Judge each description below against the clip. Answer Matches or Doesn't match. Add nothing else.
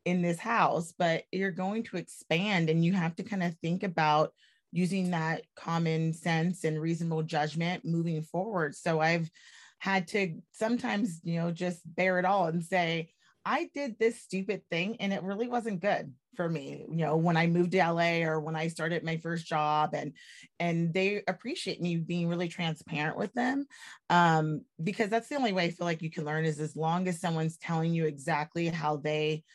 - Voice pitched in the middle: Matches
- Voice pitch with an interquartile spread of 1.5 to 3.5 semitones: Matches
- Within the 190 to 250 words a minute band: Matches